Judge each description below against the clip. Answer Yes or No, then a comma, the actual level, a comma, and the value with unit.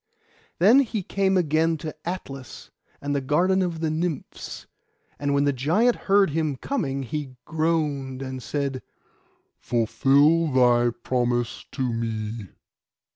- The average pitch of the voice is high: No, medium, 145 Hz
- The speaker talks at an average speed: No, slow, 130 wpm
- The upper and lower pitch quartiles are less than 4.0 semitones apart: No, average, 4.4 semitones